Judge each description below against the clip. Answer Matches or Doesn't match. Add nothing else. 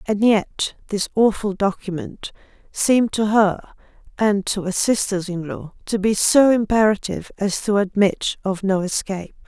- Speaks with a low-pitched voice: Doesn't match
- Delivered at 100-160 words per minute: Matches